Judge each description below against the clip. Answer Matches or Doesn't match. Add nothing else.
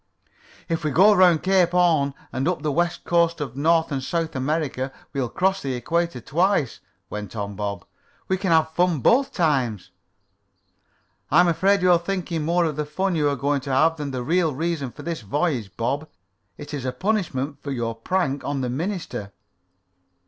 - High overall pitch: Doesn't match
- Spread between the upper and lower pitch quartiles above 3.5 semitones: Matches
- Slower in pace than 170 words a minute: Doesn't match